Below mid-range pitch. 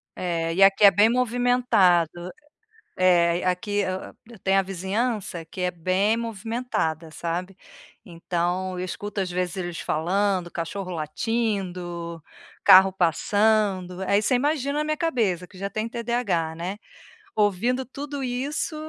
No: high, 190 Hz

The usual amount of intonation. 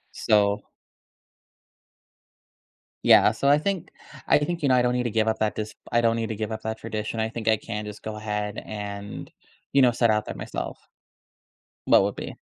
No: narrow, 2.0 semitones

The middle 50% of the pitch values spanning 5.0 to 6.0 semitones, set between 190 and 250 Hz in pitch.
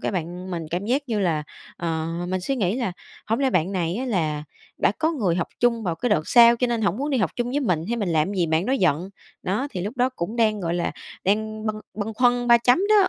Yes: wide, 5.6 semitones; high, 210 Hz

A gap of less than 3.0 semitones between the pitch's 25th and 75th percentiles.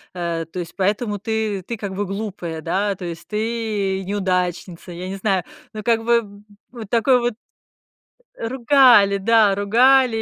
No: average, 3.3 semitones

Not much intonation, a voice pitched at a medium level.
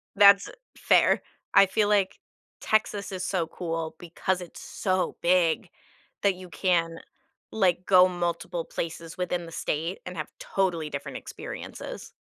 Yes: narrow, 2.3 semitones; medium, 180 Hz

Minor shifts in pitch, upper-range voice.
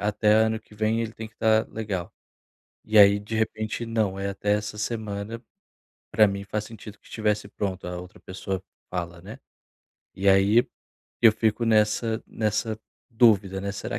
No: narrow, 1.9 semitones; low, 105 Hz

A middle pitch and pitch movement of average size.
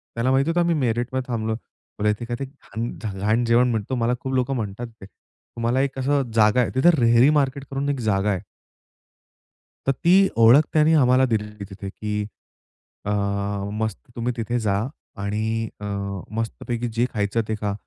No: low, 120 Hz; average, 3.4 semitones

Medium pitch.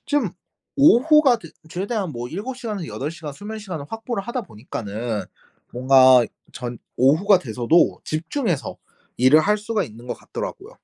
Yes: medium, 170 Hz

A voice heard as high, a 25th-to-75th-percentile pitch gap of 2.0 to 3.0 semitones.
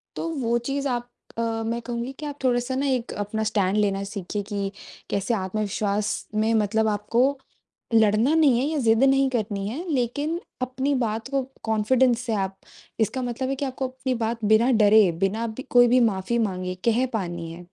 No: high, 230 Hz; average, 3.6 semitones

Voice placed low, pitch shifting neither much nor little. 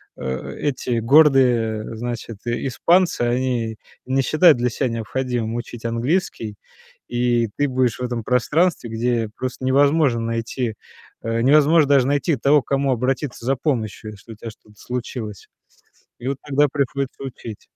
Yes: low, 125 Hz; average, 3.1 semitones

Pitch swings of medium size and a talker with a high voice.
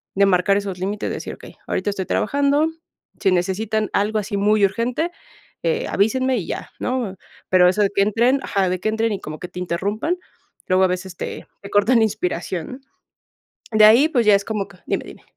Yes: average, 3.3 semitones; high, 205 Hz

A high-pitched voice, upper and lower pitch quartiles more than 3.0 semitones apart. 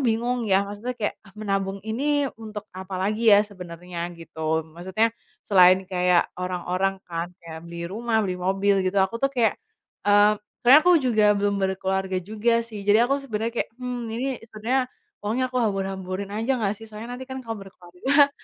Yes: high, 205 Hz; average, 3.6 semitones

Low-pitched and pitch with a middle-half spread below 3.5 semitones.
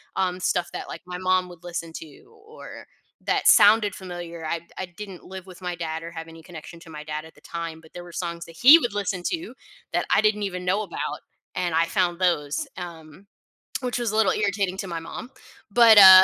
No: medium, 180 Hz; average, 2.9 semitones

